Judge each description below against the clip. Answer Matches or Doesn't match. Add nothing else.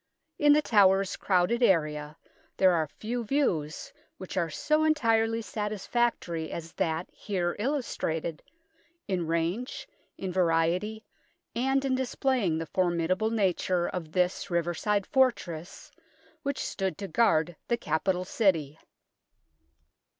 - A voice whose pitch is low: Doesn't match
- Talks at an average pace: Doesn't match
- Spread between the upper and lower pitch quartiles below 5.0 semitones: Doesn't match